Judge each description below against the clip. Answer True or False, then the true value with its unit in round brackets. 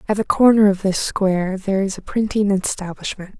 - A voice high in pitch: True (195 Hz)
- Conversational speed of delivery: True (195 wpm)